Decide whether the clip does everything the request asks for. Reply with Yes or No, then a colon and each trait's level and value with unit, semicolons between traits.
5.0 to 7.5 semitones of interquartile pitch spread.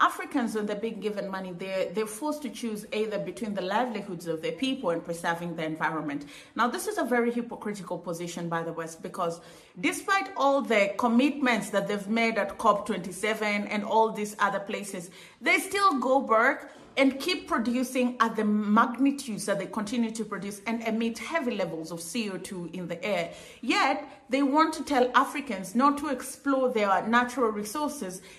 Yes: wide, 5.5 semitones